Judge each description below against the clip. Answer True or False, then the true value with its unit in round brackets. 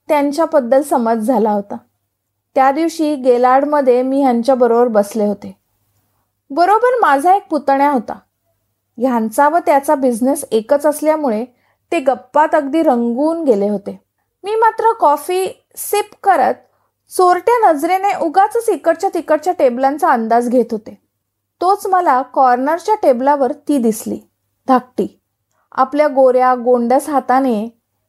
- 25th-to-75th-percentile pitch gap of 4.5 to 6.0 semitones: True (5.3 semitones)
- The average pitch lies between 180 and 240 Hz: False (275 Hz)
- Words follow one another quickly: False (120 wpm)